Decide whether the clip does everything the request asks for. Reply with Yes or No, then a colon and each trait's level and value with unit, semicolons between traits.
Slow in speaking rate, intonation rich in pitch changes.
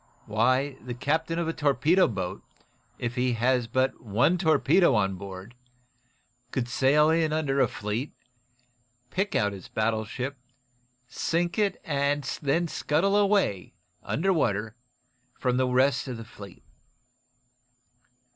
Yes: slow, 130 wpm; wide, 5.7 semitones